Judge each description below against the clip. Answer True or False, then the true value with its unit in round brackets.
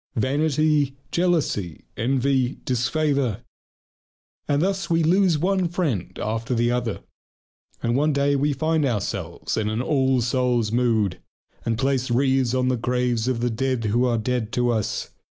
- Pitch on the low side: True (130 Hz)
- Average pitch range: True (3.5 semitones)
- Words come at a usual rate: True (150 wpm)